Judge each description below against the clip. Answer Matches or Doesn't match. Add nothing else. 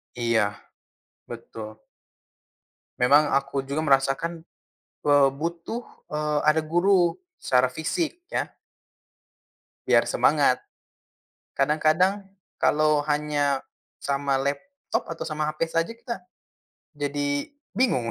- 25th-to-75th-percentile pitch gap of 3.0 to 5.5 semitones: Matches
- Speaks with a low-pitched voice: Doesn't match